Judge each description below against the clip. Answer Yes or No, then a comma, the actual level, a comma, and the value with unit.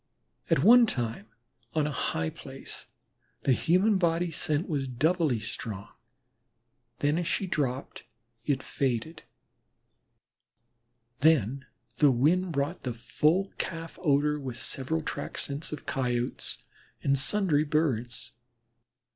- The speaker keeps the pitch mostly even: No, average, 4.6 semitones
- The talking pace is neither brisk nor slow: No, slow, 115 wpm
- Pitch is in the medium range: Yes, medium, 145 Hz